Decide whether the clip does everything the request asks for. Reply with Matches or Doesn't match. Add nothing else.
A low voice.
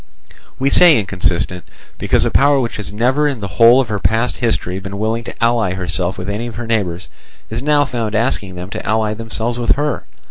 Matches